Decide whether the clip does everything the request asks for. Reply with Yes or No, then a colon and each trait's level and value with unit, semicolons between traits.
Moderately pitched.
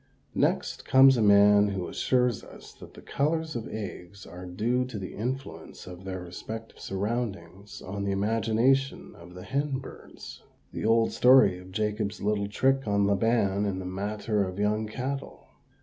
No: low, 105 Hz